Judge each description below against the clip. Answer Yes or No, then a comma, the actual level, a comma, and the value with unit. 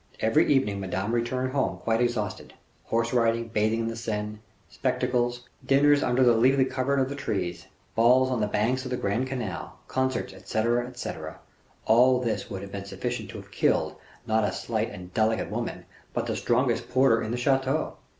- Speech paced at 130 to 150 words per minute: No, average, 180 wpm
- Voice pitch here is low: Yes, low, 120 Hz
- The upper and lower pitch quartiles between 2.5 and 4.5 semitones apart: Yes, average, 3.0 semitones